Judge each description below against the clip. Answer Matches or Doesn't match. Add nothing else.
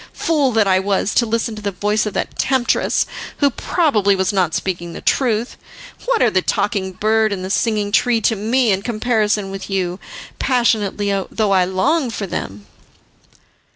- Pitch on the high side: Matches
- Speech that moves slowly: Doesn't match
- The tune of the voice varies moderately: Matches